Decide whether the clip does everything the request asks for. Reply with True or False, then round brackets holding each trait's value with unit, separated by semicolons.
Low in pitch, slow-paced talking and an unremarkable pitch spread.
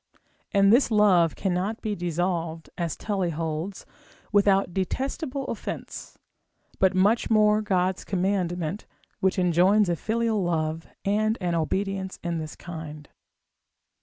False (185 Hz; 120 wpm; 3.4 semitones)